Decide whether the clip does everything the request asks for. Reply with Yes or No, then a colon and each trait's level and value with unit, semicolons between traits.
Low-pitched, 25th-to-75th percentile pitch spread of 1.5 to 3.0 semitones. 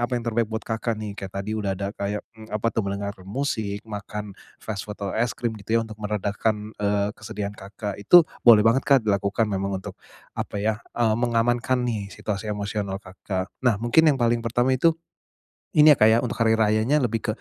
Yes: low, 110 Hz; narrow, 2.5 semitones